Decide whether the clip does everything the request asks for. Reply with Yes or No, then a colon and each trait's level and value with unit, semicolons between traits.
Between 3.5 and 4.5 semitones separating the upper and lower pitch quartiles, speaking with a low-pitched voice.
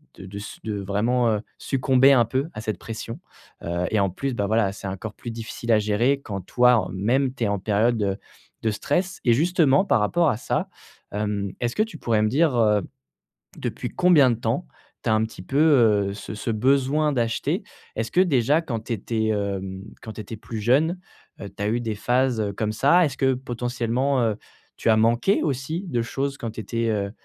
Yes: average, 4.0 semitones; low, 115 Hz